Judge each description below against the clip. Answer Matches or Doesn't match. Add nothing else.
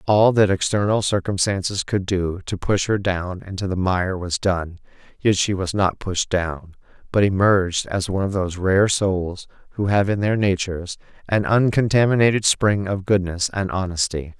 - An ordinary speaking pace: Matches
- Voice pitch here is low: Matches